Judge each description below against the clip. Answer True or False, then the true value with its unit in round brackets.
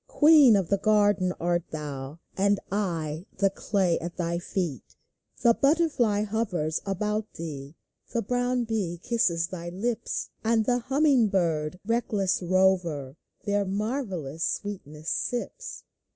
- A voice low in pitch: False (195 Hz)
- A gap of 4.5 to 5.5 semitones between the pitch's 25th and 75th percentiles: True (5.0 semitones)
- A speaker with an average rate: False (125 wpm)